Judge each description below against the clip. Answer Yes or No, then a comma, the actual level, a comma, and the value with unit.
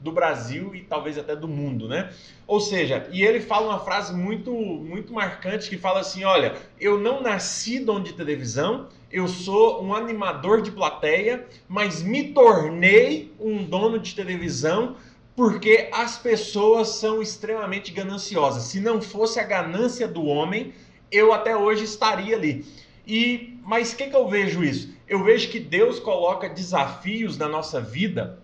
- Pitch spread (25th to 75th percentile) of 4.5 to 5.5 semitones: No, average, 3.9 semitones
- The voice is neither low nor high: No, high, 205 Hz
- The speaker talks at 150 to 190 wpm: Yes, average, 160 wpm